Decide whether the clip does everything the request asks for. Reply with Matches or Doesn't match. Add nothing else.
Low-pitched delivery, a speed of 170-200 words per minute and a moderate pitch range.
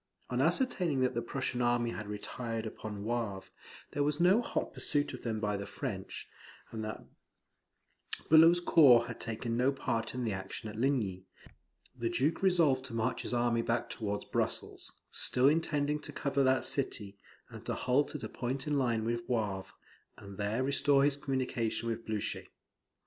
Matches